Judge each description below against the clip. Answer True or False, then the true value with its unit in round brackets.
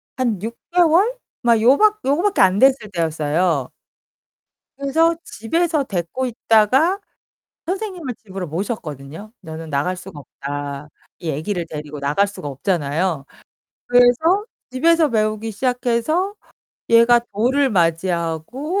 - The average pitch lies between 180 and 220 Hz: True (215 Hz)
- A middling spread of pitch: False (8.9 semitones)